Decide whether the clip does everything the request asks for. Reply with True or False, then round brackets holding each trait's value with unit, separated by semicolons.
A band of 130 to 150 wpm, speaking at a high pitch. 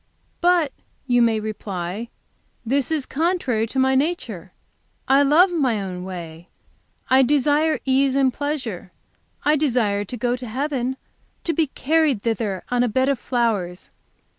True (145 wpm; 255 Hz)